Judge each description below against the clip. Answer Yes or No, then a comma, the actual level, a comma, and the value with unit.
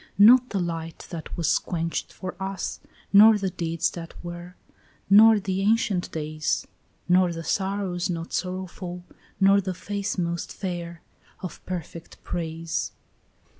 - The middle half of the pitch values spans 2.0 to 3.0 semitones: Yes, narrow, 2.6 semitones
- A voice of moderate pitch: Yes, medium, 180 Hz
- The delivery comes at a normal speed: No, slow, 130 wpm